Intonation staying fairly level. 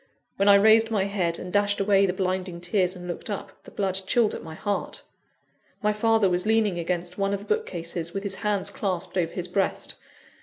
Yes: narrow, 2.3 semitones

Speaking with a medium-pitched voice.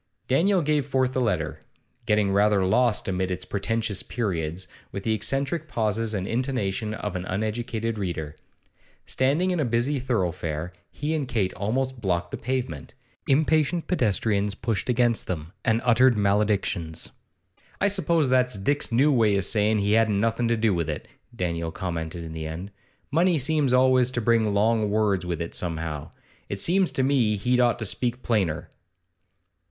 No: low, 110 Hz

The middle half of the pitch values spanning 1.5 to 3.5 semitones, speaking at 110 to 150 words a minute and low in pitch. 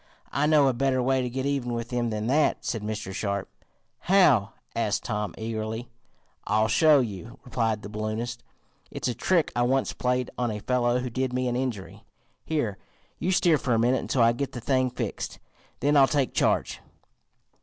No: average, 3.0 semitones; average, 185 wpm; low, 120 Hz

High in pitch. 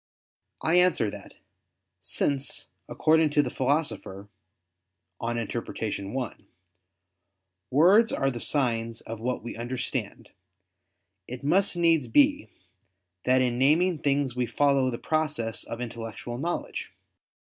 No: low, 130 Hz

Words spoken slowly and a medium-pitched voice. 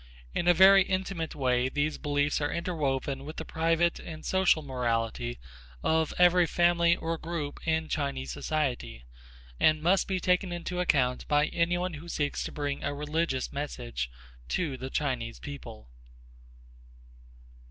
No: average, 145 wpm; medium, 155 Hz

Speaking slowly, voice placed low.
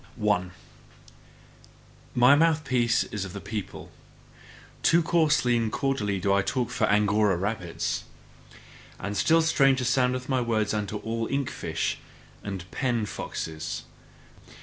Yes: slow, 125 wpm; low, 115 Hz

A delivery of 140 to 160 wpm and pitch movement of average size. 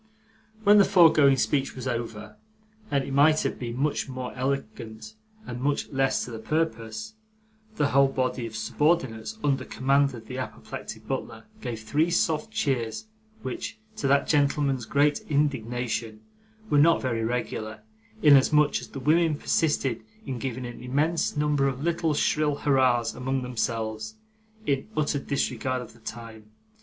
Yes: average, 150 wpm; average, 3.8 semitones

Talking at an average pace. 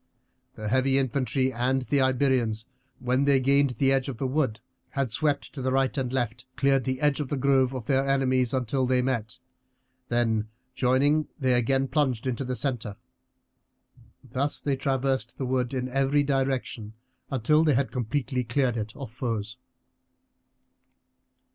Yes: average, 160 wpm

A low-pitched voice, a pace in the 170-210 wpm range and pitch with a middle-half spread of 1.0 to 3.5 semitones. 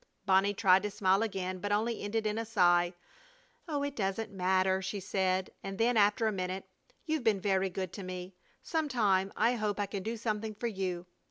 No: high, 200 Hz; average, 200 wpm; average, 2.8 semitones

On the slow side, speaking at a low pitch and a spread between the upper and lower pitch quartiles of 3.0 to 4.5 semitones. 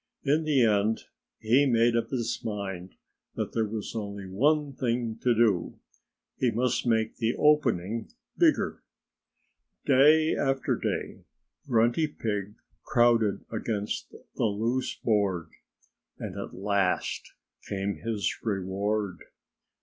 Yes: slow, 115 wpm; low, 115 Hz; average, 3.6 semitones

